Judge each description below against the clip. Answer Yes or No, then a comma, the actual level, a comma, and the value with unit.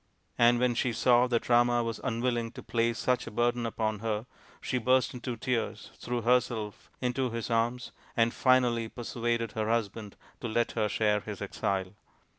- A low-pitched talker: Yes, low, 120 Hz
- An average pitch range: No, narrow, 1.5 semitones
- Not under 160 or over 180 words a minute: Yes, average, 175 wpm